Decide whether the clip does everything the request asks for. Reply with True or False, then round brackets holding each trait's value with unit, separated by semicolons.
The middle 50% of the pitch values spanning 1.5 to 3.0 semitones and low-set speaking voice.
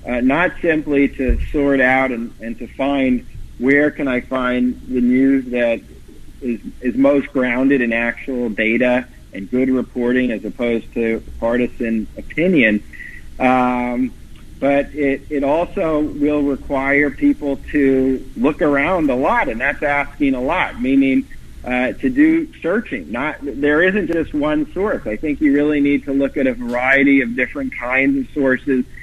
True (2.6 semitones; 130 Hz)